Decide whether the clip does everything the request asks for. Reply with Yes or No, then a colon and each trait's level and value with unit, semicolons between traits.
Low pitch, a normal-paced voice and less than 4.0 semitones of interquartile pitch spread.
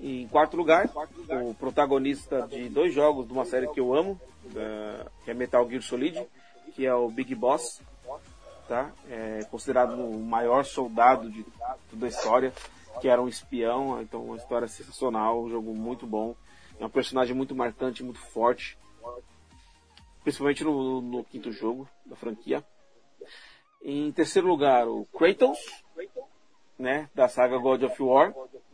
Yes: low, 125 Hz; average, 145 wpm; average, 2.9 semitones